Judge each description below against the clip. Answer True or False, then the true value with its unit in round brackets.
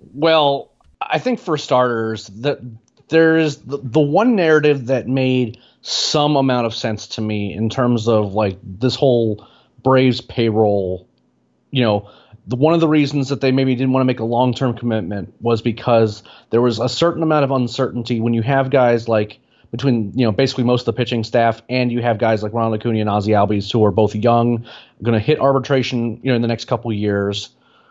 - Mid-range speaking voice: False (120 Hz)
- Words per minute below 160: False (200 wpm)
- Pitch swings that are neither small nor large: True (3.3 semitones)